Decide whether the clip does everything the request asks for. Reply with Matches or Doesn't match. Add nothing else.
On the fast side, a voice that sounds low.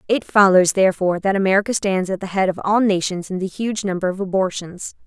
Doesn't match